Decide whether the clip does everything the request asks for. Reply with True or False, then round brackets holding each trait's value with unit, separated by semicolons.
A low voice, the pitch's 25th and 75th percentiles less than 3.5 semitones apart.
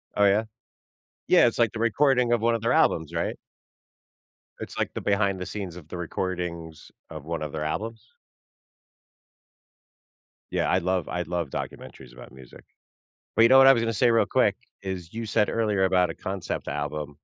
False (95 Hz; 5.3 semitones)